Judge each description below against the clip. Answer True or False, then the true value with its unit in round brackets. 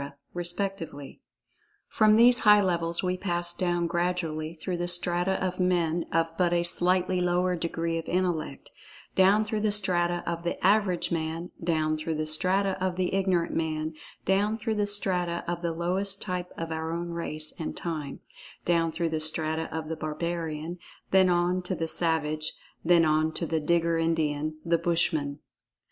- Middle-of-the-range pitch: True (170 Hz)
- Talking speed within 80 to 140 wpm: False (160 wpm)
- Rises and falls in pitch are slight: True (2.1 semitones)